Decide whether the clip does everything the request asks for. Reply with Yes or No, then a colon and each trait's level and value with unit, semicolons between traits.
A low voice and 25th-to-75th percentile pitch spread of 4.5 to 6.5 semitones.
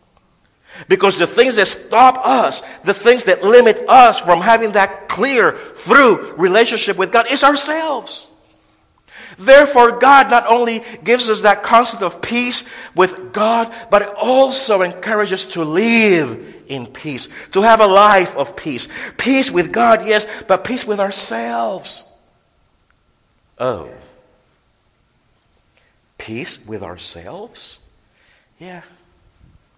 No: high, 210 Hz; average, 5.2 semitones